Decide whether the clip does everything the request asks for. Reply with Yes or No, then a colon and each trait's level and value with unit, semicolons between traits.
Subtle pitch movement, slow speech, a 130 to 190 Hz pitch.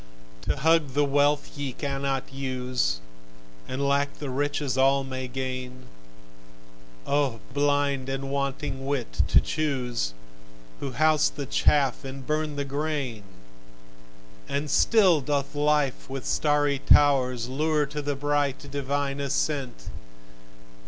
Yes: narrow, 1.7 semitones; slow, 120 wpm; medium, 140 Hz